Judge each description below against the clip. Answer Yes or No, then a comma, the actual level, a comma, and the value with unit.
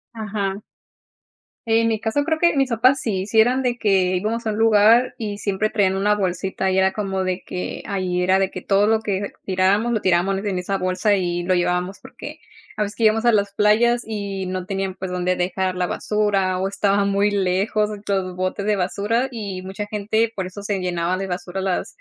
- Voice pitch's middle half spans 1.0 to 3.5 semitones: Yes, narrow, 2.5 semitones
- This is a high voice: Yes, high, 200 Hz